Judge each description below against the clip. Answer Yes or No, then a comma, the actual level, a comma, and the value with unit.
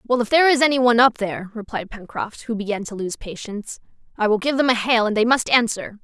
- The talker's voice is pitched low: No, high, 230 Hz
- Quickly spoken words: Yes, fast, 250 wpm